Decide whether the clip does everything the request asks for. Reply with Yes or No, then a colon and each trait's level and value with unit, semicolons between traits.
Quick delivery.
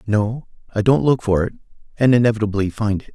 No: average, 155 wpm